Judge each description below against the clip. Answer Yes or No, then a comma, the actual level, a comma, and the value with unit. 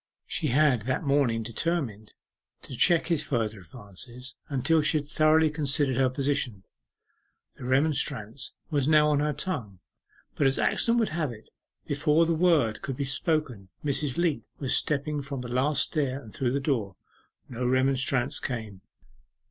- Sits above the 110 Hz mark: Yes, low, 135 Hz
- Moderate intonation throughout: Yes, average, 3.5 semitones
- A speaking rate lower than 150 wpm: No, average, 155 wpm